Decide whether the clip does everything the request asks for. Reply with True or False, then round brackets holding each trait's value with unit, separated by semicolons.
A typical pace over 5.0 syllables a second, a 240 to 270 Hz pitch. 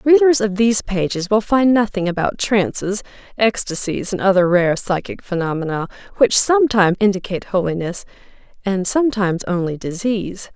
False (5.5 syllables/s; 200 Hz)